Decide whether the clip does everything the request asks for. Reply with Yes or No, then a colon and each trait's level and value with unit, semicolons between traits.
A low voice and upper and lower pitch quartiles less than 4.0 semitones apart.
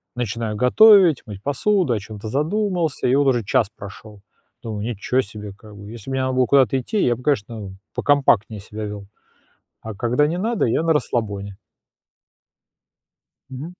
No: low, 120 Hz; wide, 5.4 semitones